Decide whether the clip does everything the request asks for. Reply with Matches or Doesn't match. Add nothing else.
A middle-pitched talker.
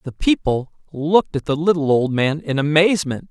Matches